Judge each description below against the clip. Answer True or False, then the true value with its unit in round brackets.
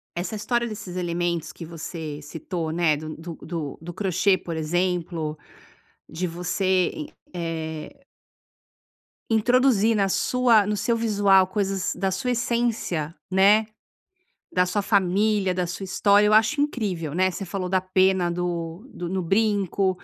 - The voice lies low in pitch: False (185 Hz)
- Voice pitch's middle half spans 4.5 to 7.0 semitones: False (3.5 semitones)